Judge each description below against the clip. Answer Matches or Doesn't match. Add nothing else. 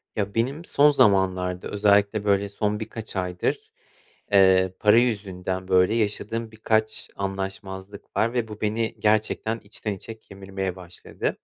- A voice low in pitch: Matches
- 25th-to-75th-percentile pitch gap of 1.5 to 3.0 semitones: Matches